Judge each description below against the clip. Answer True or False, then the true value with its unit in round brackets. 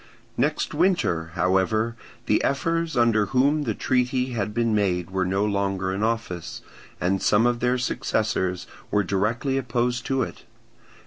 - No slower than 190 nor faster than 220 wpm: False (145 wpm)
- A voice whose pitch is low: True (110 Hz)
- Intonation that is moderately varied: True (4.4 semitones)